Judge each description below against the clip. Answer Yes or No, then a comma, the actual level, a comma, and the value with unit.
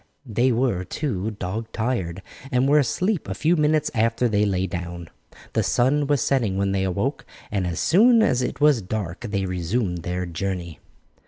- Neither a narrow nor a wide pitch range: No, wide, 6.3 semitones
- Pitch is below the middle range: Yes, low, 110 Hz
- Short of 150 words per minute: No, average, 175 wpm